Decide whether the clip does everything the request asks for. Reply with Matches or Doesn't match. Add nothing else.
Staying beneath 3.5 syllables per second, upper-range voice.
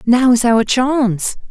Matches